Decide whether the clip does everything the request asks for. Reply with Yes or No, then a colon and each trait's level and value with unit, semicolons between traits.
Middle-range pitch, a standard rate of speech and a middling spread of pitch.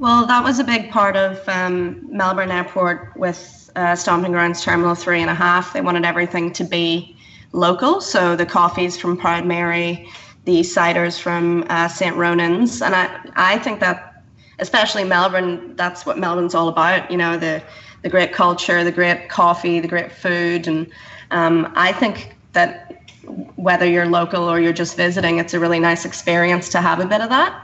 No: medium, 175 Hz; average, 180 wpm; narrow, 0.9 semitones